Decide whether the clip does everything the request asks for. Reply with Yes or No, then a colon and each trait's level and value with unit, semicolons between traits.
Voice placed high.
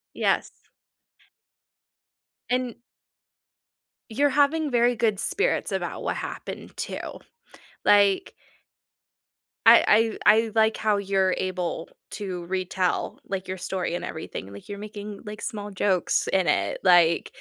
Yes: high, 200 Hz